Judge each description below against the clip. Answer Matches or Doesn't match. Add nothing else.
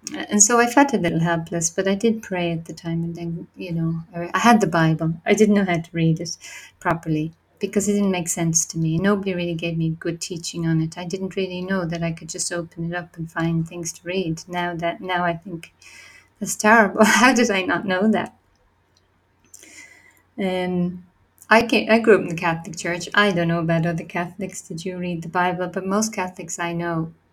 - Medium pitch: Matches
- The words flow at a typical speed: Doesn't match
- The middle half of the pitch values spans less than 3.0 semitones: Matches